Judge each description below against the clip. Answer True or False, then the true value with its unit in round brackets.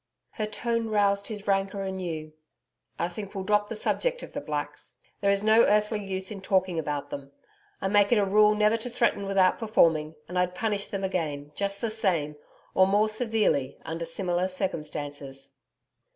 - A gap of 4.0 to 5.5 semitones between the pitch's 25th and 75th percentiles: False (3.6 semitones)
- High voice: True (195 Hz)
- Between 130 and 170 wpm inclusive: False (180 wpm)